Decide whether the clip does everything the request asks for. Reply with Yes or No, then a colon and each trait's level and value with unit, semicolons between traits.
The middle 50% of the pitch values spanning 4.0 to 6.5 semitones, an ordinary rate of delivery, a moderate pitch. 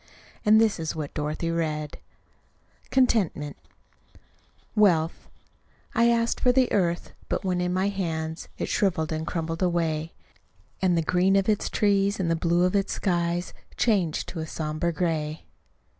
No: average, 3.6 semitones; average, 150 wpm; medium, 175 Hz